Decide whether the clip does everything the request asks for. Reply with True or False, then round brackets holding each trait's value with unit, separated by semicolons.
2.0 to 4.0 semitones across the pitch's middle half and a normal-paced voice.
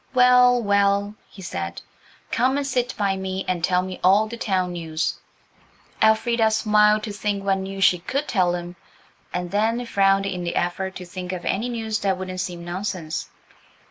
True (3.2 semitones; 175 wpm)